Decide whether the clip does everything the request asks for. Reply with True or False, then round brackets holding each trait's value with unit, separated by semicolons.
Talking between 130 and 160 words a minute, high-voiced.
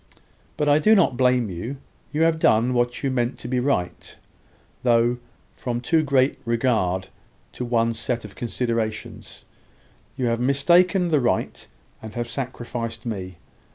False (150 wpm; 120 Hz)